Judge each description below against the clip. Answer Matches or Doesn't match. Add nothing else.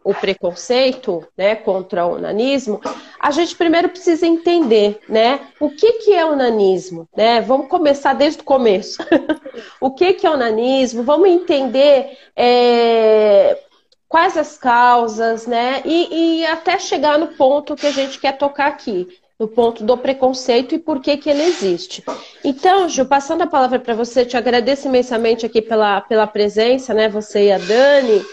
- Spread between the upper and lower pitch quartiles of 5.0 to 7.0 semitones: Matches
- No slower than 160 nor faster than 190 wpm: Matches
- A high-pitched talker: Matches